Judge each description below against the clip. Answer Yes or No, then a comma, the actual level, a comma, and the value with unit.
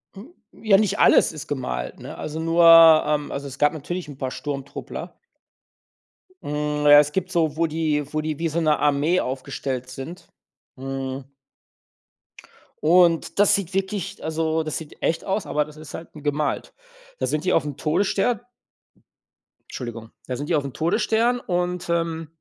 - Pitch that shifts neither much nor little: Yes, average, 3.0 semitones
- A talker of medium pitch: Yes, medium, 155 Hz